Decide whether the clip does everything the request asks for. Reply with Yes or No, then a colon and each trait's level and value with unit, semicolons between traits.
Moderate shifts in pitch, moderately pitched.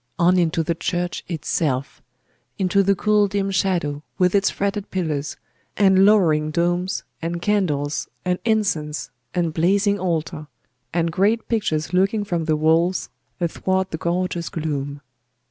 Yes: average, 3.6 semitones; medium, 175 Hz